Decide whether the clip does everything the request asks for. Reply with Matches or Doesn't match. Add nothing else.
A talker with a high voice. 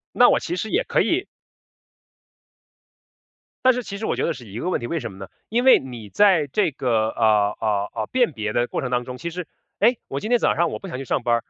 Doesn't match